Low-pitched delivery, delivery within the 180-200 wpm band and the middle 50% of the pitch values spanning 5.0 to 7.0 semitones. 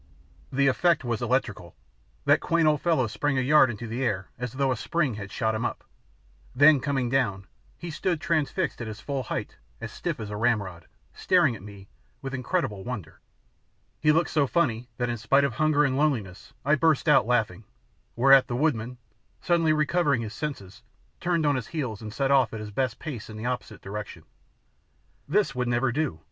Yes: low, 130 Hz; average, 190 wpm; wide, 5.4 semitones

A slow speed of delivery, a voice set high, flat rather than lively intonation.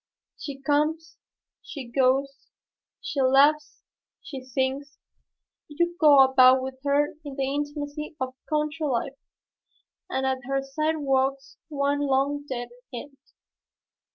Yes: slow, 115 wpm; very high, 275 Hz; narrow, 1.8 semitones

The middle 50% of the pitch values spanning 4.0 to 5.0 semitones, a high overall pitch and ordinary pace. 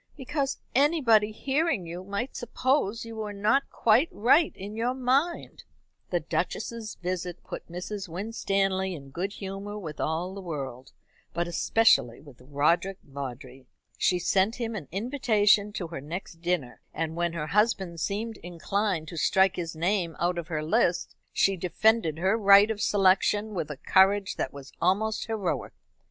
Yes: average, 4.6 semitones; high, 195 Hz; average, 155 wpm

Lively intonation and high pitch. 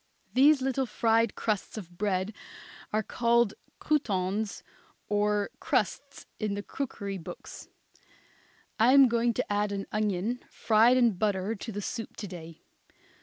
No: average, 2.9 semitones; high, 215 Hz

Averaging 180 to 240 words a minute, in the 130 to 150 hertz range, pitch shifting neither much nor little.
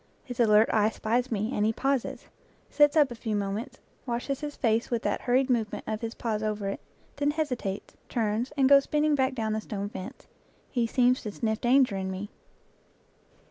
No: average, 195 wpm; high, 230 Hz; average, 3.5 semitones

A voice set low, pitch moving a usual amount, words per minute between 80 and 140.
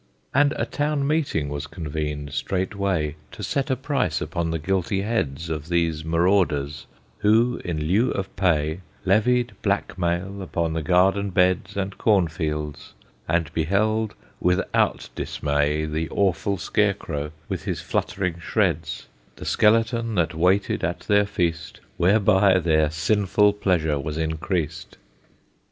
Yes: very low, 90 Hz; average, 4.4 semitones; slow, 135 wpm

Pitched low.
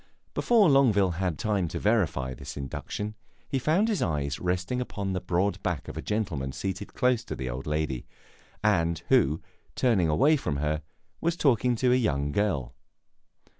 Yes: very low, 95 Hz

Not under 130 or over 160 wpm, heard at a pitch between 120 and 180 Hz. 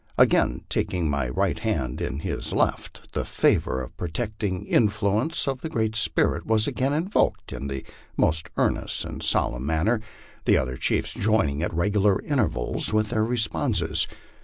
No: average, 155 wpm; low, 105 Hz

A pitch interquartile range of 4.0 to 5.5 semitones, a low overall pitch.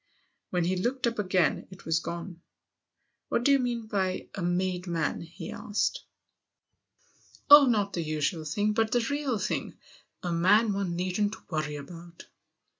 No: average, 4.4 semitones; medium, 185 Hz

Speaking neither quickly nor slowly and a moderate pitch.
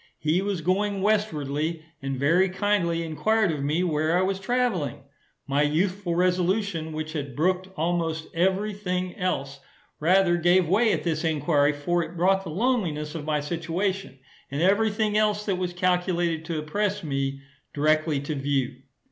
Yes: average, 160 wpm; medium, 175 Hz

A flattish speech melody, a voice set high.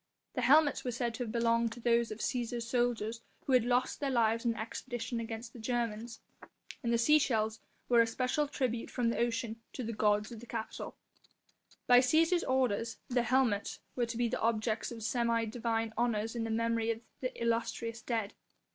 Yes: narrow, 1.5 semitones; high, 235 Hz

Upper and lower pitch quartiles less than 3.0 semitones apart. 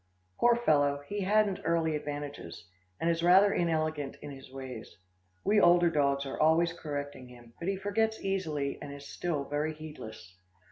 No: average, 3.9 semitones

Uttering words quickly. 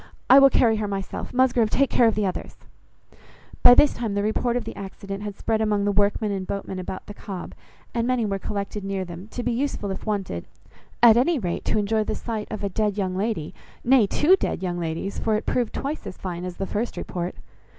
Yes: fast, 225 wpm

